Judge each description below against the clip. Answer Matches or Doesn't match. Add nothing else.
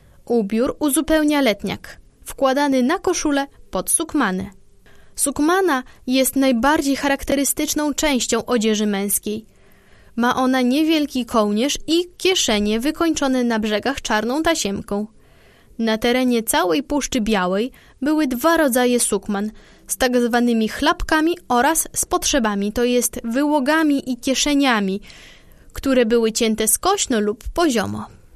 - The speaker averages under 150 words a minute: Matches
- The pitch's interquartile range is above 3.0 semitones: Matches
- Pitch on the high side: Matches